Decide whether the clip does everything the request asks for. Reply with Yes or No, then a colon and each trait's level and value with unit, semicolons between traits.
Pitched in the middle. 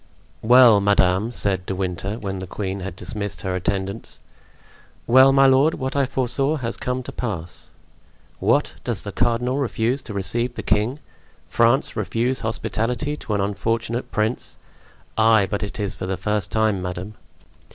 No: low, 110 Hz